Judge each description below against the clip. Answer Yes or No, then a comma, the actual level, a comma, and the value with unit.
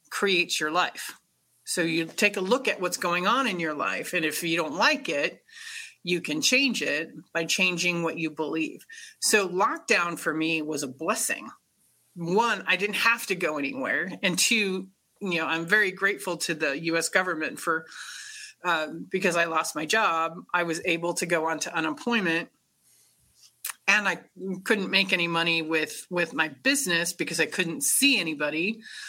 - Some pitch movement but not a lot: Yes, average, 4.0 semitones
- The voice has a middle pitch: Yes, medium, 175 Hz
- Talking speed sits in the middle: Yes, average, 175 wpm